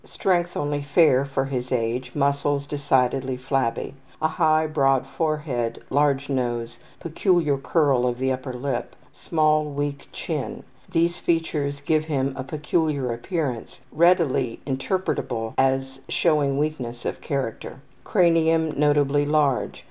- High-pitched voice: No, medium, 140 Hz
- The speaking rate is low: Yes, slow, 125 wpm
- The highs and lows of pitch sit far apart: No, average, 2.9 semitones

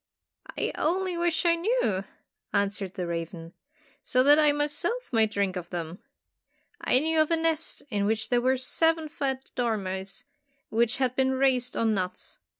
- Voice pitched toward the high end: Yes, very high, 255 Hz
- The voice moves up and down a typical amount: No, wide, 7.6 semitones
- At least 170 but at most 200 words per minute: No, average, 155 wpm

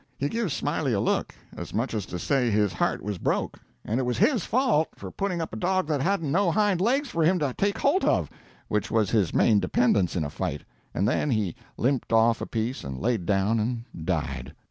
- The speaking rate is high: Yes, fast, 225 wpm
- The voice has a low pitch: Yes, low, 125 Hz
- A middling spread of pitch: No, wide, 9.0 semitones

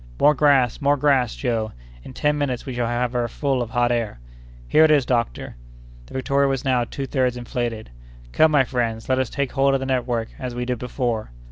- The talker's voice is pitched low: Yes, low, 125 Hz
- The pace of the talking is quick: Yes, fast, 215 wpm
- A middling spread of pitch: No, narrow, 2.3 semitones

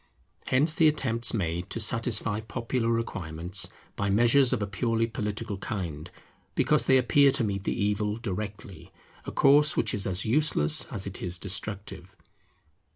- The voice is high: No, low, 105 Hz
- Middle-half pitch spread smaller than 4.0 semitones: Yes, average, 3.4 semitones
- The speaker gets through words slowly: No, average, 155 wpm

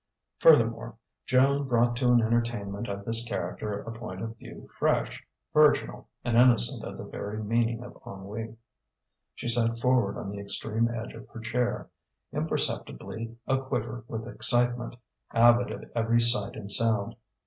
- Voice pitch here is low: Yes, low, 115 Hz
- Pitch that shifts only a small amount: Yes, narrow, 1.6 semitones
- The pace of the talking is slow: No, average, 150 wpm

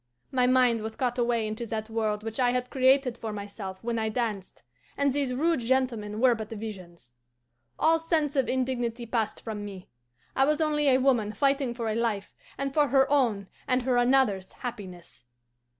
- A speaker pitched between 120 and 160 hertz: No, high, 240 Hz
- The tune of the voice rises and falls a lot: No, average, 3.5 semitones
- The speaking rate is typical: Yes, average, 180 wpm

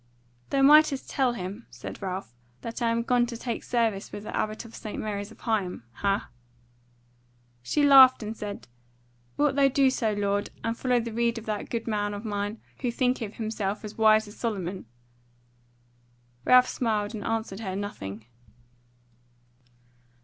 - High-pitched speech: Yes, high, 220 Hz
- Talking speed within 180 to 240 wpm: No, average, 155 wpm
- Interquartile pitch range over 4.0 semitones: No, average, 2.8 semitones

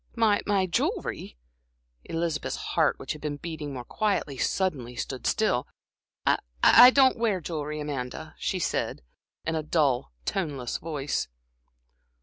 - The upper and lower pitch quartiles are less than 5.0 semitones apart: No, wide, 5.6 semitones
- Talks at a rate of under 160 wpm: Yes, slow, 135 wpm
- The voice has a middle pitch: Yes, medium, 155 Hz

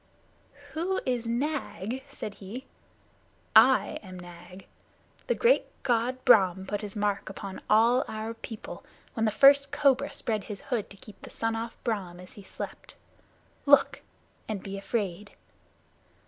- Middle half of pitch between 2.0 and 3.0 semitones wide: No, average, 4.4 semitones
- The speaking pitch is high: Yes, high, 220 Hz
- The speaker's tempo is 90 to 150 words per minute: Yes, average, 145 wpm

